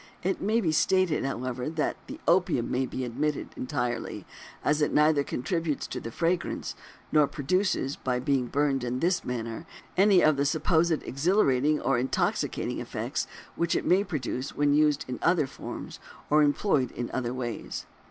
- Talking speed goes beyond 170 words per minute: No, average, 160 wpm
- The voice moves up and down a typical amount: Yes, average, 4.7 semitones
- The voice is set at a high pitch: No, medium, 145 Hz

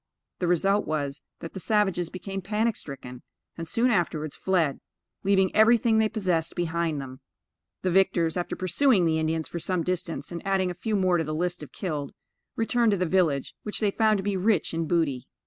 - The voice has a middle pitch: Yes, medium, 180 Hz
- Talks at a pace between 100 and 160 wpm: No, average, 195 wpm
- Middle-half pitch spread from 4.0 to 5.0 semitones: No, average, 3.6 semitones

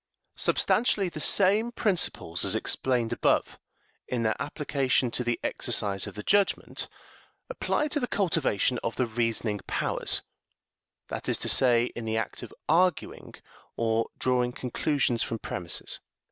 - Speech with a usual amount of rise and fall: No, wide, 7.0 semitones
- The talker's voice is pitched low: Yes, low, 125 Hz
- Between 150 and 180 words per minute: No, average, 140 wpm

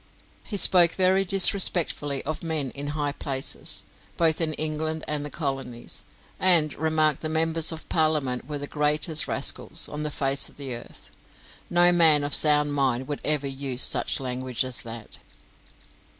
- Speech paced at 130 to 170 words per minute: Yes, average, 160 wpm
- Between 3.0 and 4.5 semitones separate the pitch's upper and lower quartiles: No, narrow, 2.6 semitones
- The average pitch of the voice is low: No, medium, 150 Hz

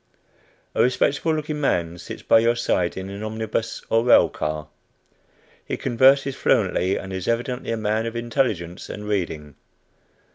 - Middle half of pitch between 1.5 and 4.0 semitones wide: No, average, 4.7 semitones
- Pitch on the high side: No, low, 110 Hz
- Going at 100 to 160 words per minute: Yes, average, 150 wpm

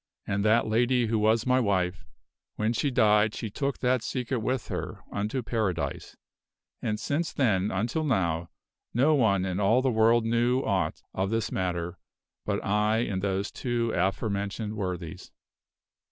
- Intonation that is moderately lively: Yes, average, 3.7 semitones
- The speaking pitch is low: Yes, low, 110 Hz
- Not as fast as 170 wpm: Yes, average, 155 wpm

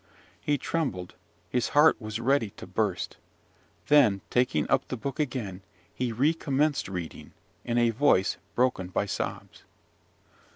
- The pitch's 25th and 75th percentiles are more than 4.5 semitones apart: Yes, average, 5.1 semitones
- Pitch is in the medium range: No, low, 125 Hz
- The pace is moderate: No, slow, 130 wpm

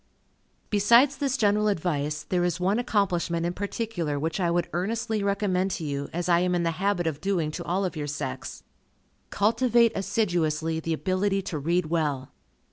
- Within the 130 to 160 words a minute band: No, average, 175 wpm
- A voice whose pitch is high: No, medium, 180 Hz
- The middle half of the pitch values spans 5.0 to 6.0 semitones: No, average, 3.9 semitones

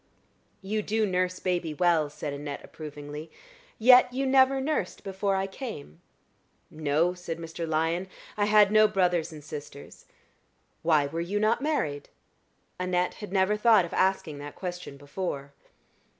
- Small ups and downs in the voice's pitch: No, average, 5.2 semitones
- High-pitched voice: No, medium, 180 Hz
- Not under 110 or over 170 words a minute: Yes, average, 145 wpm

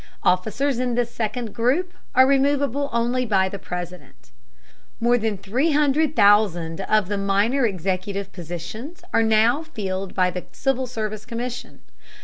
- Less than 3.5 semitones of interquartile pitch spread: No, average, 4.7 semitones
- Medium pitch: No, high, 220 Hz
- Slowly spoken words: Yes, slow, 130 wpm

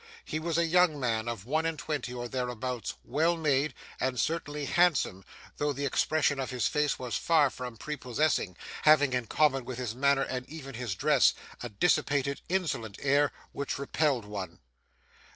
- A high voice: No, medium, 140 Hz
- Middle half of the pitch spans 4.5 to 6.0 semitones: No, average, 3.7 semitones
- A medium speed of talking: Yes, average, 170 wpm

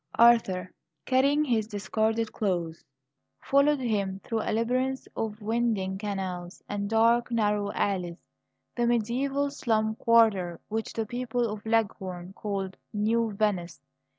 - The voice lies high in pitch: Yes, high, 220 Hz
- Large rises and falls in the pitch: No, average, 3.1 semitones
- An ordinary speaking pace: No, slow, 125 wpm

